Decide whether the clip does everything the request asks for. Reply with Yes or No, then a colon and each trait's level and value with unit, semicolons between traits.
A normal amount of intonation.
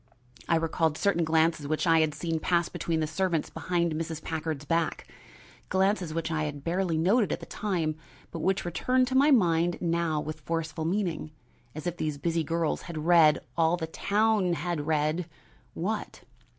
No: narrow, 2.0 semitones